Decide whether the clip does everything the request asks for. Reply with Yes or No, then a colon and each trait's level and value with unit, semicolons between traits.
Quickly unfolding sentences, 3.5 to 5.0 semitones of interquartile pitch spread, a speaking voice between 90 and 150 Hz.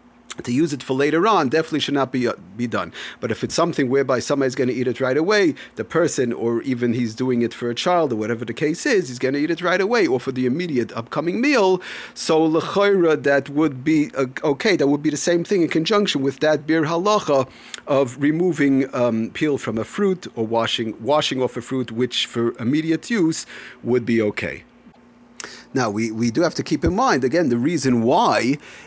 Yes: fast, 220 wpm; average, 4.7 semitones; low, 135 Hz